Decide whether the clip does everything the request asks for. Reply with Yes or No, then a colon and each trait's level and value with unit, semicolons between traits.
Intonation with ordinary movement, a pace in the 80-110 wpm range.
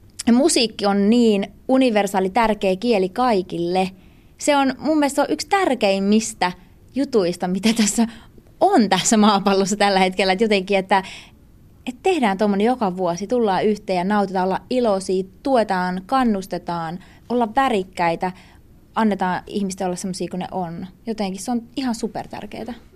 No: average, 4.0 semitones; average, 140 wpm